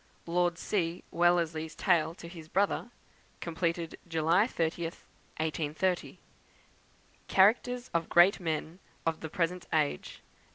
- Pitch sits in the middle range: Yes, medium, 170 Hz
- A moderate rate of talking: No, slow, 115 wpm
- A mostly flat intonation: Yes, narrow, 1.9 semitones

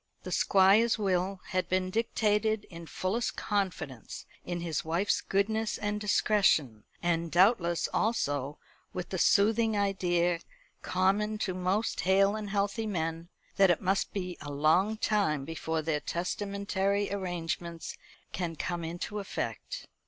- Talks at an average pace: No, slow, 130 wpm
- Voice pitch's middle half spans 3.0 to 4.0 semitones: Yes, average, 3.3 semitones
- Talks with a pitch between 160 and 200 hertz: Yes, high, 190 Hz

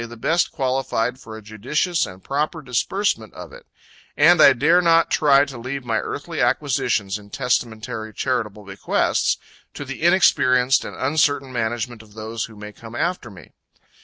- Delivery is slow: No, average, 165 wpm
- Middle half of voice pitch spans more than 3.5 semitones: Yes, average, 4.6 semitones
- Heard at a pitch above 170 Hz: No, low, 125 Hz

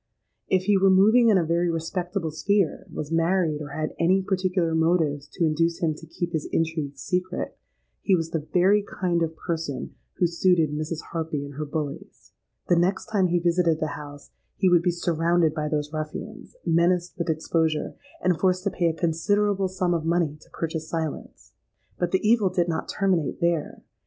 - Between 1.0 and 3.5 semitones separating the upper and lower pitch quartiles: Yes, narrow, 2.5 semitones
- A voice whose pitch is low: No, medium, 170 Hz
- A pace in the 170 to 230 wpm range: Yes, average, 185 wpm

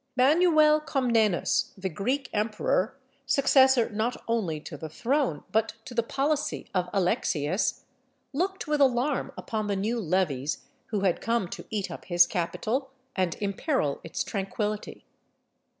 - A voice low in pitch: No, high, 220 Hz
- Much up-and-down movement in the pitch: Yes, wide, 6.1 semitones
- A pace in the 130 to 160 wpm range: Yes, average, 140 wpm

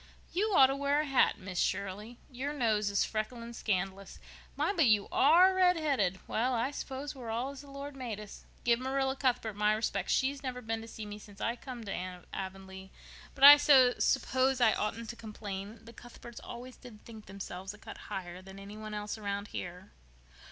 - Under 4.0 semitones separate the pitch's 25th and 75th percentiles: No, average, 4.7 semitones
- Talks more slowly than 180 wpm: No, average, 195 wpm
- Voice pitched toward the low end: No, high, 230 Hz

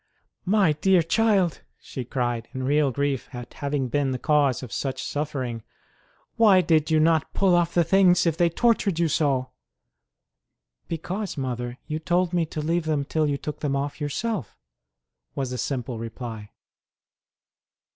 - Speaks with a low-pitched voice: No, medium, 150 Hz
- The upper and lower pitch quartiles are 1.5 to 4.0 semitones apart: No, average, 4.7 semitones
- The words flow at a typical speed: Yes, average, 155 wpm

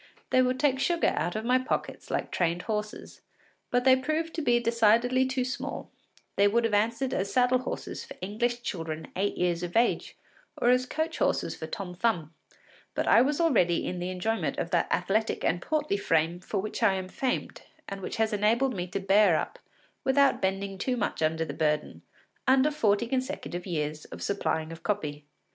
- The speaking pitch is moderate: No, high, 215 Hz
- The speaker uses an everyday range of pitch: No, wide, 6.1 semitones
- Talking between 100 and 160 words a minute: No, average, 190 wpm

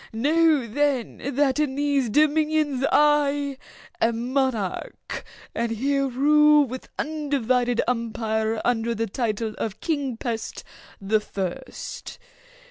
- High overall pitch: Yes, very high, 260 Hz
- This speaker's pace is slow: Yes, slow, 110 wpm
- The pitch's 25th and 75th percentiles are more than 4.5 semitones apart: No, average, 4.2 semitones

